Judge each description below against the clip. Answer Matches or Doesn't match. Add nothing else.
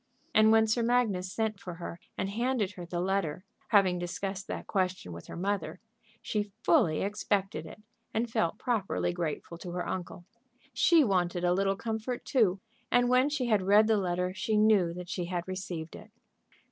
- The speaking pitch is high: Matches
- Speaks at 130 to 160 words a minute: Doesn't match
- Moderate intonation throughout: Matches